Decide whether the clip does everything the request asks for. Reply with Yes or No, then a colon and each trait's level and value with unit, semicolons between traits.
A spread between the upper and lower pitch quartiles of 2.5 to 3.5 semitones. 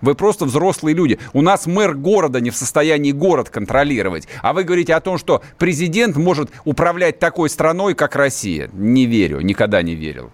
No: wide, 5.5 semitones